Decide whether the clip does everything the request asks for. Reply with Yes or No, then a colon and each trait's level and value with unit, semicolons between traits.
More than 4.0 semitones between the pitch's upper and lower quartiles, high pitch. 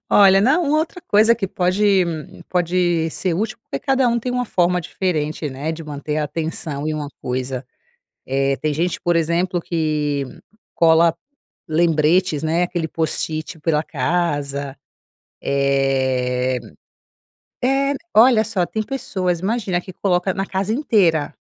No: average, 4.5 semitones; medium, 170 Hz